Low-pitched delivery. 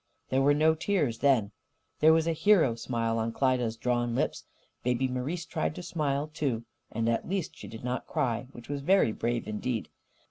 Yes: low, 125 Hz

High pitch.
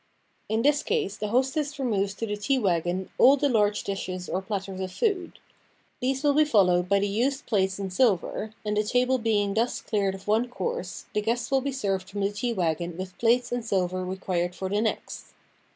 Yes: high, 210 Hz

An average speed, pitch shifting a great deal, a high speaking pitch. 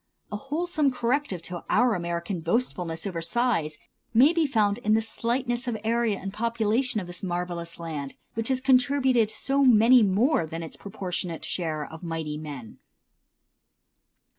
Yes: average, 150 wpm; wide, 6.5 semitones; high, 215 Hz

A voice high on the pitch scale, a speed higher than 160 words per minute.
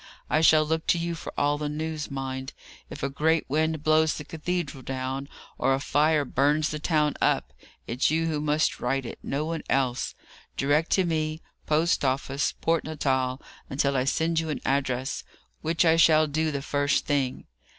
No: medium, 150 Hz; average, 185 wpm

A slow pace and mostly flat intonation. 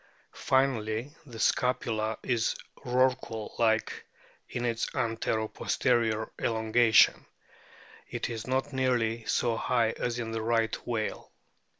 Yes: slow, 110 wpm; narrow, 1.8 semitones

